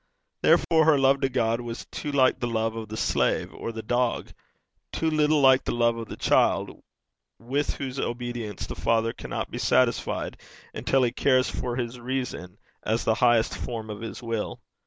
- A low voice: Yes, low, 120 Hz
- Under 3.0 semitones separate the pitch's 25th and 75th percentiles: Yes, narrow, 2.6 semitones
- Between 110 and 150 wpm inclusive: No, average, 180 wpm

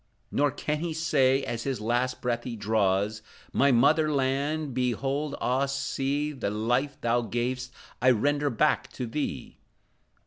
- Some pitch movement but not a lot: Yes, average, 3.3 semitones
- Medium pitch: No, low, 130 Hz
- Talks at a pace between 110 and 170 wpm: Yes, average, 145 wpm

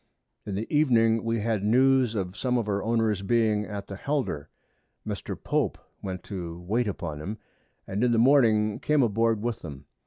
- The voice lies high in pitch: No, low, 110 Hz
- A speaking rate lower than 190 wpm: Yes, average, 180 wpm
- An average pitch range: Yes, average, 3.2 semitones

